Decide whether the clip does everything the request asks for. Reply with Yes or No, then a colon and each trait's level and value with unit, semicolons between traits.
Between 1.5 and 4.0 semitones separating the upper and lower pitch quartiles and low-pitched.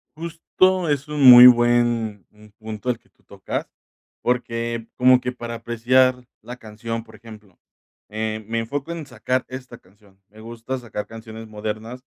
Yes: narrow, 2.4 semitones; low, 120 Hz